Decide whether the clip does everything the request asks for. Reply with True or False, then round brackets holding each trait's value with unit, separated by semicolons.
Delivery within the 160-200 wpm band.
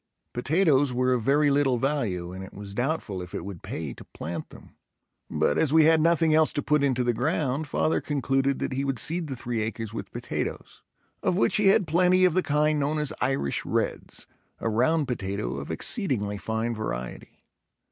True (195 wpm)